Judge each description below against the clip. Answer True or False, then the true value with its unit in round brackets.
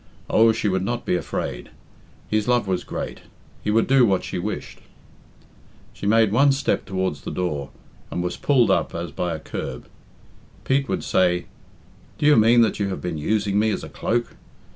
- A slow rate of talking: False (185 wpm)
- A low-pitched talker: True (105 Hz)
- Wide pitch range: False (4.4 semitones)